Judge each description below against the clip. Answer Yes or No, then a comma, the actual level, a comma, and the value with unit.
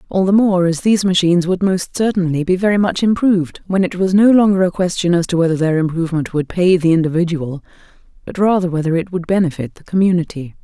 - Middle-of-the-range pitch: Yes, medium, 180 Hz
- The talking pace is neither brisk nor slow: No, fast, 210 wpm